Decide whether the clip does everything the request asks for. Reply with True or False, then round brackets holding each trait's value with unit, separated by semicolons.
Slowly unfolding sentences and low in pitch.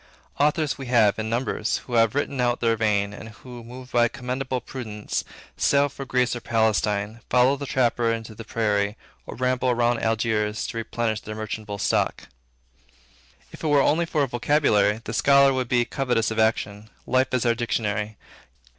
False (180 wpm; 120 Hz)